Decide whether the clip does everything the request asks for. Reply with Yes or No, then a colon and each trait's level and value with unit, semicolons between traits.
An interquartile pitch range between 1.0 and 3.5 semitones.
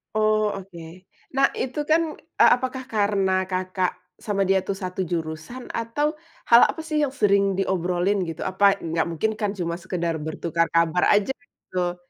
No: average, 4.5 semitones